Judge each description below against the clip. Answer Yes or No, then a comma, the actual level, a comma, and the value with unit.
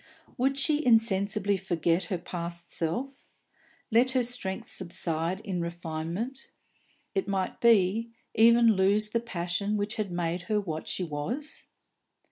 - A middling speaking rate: No, slow, 130 wpm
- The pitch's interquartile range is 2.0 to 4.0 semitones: No, average, 5.1 semitones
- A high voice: Yes, high, 195 Hz